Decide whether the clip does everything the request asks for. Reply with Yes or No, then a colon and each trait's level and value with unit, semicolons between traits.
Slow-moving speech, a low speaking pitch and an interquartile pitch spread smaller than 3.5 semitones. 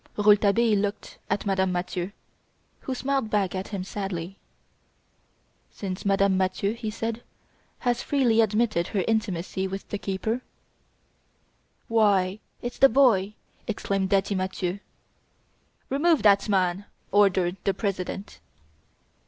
No: slow, 120 wpm; high, 200 Hz; average, 2.7 semitones